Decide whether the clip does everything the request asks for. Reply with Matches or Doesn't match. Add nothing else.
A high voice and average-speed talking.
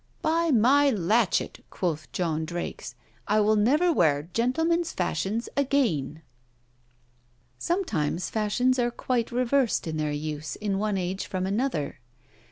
Doesn't match